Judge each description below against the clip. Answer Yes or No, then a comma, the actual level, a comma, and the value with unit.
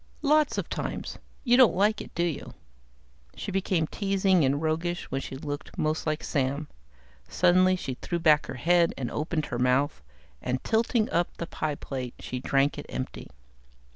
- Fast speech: No, average, 170 wpm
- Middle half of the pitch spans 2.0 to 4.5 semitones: No, average, 5.2 semitones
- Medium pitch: Yes, medium, 160 Hz